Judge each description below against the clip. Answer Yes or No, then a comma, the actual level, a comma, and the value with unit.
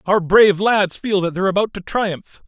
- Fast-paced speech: Yes, fast, 220 wpm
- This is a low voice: No, high, 190 Hz